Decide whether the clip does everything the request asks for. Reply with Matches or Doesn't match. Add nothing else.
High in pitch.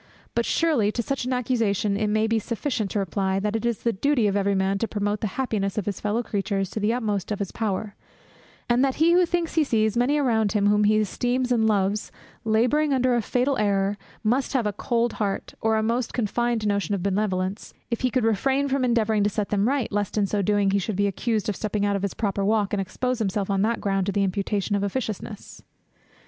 Matches